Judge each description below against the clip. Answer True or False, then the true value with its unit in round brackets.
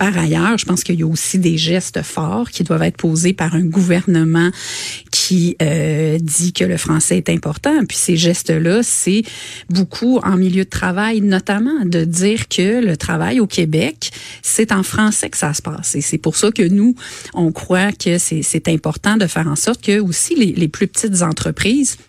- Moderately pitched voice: True (180 Hz)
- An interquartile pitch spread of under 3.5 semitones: False (3.9 semitones)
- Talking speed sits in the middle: True (200 wpm)